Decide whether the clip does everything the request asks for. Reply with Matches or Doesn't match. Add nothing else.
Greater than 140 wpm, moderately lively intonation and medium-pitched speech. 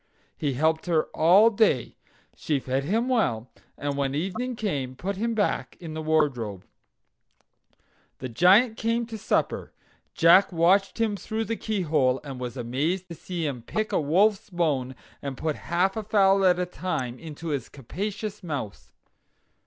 Doesn't match